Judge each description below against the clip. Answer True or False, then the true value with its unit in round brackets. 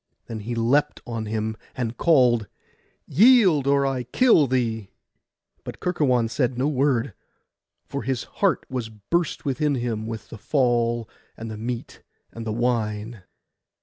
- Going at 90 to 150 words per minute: True (145 wpm)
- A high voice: False (120 Hz)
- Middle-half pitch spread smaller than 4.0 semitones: True (3.6 semitones)